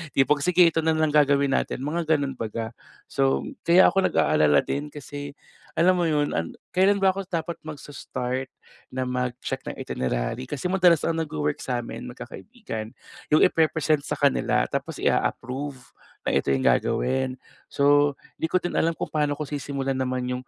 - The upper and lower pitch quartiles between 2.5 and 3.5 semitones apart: No, average, 4.2 semitones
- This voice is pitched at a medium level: Yes, medium, 145 Hz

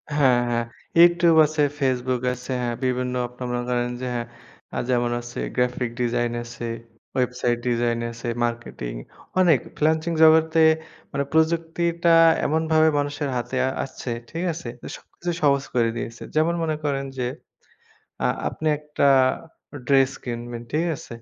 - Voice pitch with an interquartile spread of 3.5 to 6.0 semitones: Yes, average, 4.7 semitones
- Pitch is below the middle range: Yes, low, 130 Hz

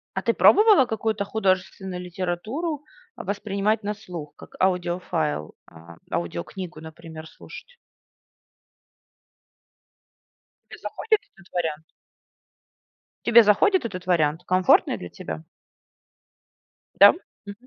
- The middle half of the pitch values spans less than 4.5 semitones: No, average, 5.1 semitones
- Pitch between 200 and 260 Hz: No, medium, 185 Hz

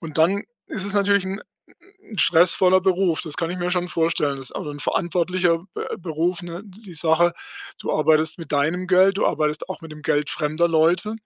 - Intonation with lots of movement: No, average, 2.7 semitones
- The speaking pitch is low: No, medium, 170 Hz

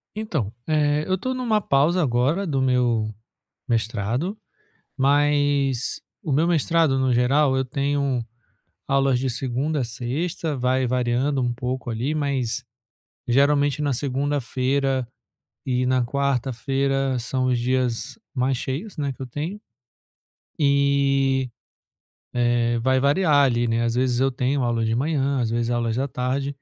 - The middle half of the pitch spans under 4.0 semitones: Yes, narrow, 2.6 semitones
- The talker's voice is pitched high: No, low, 135 Hz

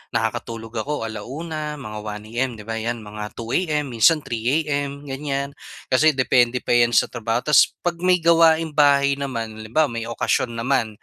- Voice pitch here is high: No, low, 130 Hz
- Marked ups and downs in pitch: No, average, 4.7 semitones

